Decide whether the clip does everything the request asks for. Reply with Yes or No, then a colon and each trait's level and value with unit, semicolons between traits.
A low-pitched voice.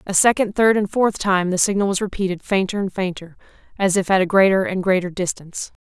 No: high, 190 Hz